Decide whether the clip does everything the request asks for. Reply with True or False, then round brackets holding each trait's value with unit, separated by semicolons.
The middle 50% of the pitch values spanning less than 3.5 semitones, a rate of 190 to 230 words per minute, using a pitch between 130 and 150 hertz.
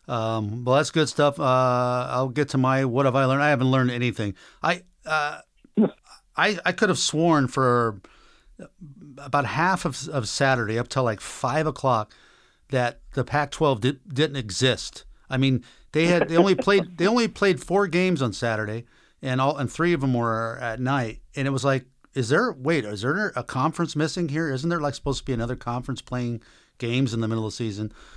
False (4.2 semitones; 200 wpm; 135 Hz)